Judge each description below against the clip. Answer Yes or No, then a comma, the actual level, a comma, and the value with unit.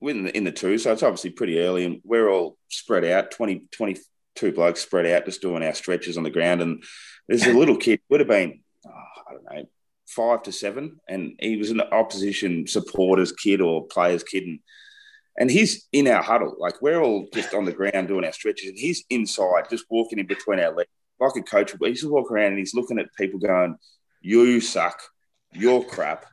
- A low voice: Yes, low, 105 Hz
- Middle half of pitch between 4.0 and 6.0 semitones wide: Yes, wide, 5.5 semitones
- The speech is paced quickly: Yes, fast, 210 wpm